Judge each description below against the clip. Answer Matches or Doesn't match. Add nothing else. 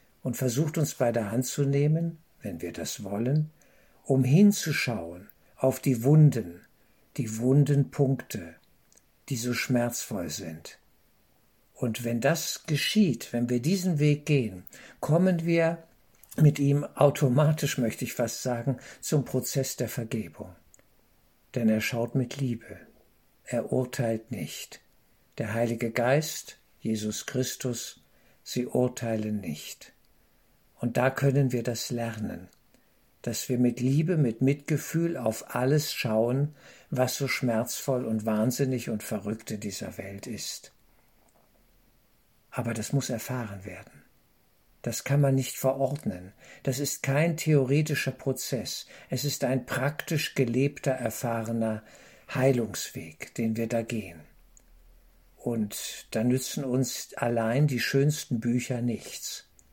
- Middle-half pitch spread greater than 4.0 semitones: Doesn't match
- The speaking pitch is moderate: Doesn't match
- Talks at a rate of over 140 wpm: Doesn't match